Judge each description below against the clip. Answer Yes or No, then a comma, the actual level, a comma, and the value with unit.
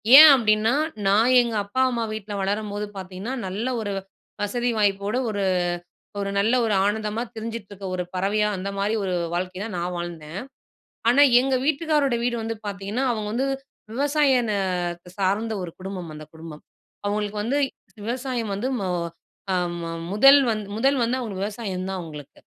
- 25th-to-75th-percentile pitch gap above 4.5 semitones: No, average, 3.7 semitones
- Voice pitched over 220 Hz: No, high, 210 Hz